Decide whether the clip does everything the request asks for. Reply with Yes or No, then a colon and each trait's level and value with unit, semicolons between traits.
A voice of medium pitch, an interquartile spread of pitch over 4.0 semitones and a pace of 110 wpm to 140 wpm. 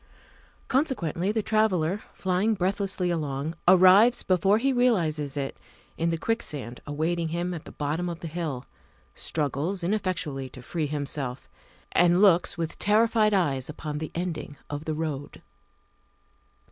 Yes: medium, 170 Hz; average, 4.5 semitones; slow, 135 wpm